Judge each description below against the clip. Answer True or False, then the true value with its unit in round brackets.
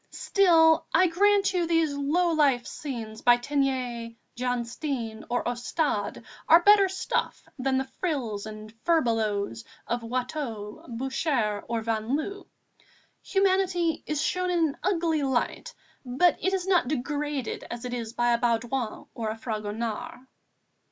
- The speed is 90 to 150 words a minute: True (140 wpm)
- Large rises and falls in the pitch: True (6.2 semitones)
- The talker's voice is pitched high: True (265 Hz)